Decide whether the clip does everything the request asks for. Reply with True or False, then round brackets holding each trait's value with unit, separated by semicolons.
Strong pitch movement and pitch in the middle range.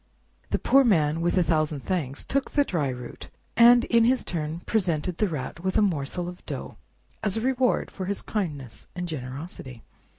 True (6.3 semitones; 175 Hz)